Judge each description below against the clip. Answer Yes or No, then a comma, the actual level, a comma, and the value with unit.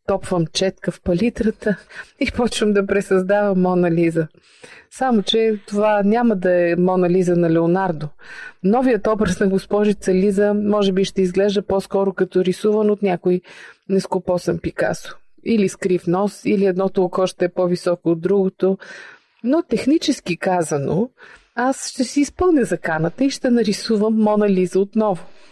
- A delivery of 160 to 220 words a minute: No, average, 145 wpm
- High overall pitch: Yes, high, 195 Hz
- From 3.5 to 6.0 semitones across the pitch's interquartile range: No, average, 2.7 semitones